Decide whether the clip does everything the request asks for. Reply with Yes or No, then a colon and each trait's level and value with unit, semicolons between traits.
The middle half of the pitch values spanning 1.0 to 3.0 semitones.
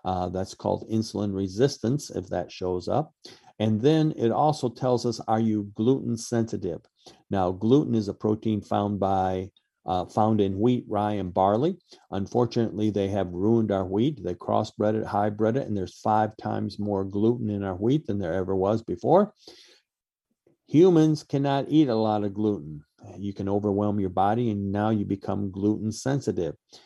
Yes: average, 2.7 semitones